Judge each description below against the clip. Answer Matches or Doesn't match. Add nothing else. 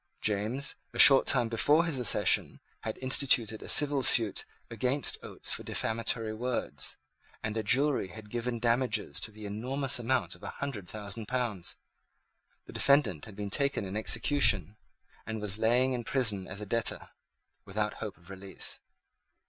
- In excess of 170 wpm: Doesn't match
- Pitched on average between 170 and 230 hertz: Doesn't match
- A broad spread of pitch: Doesn't match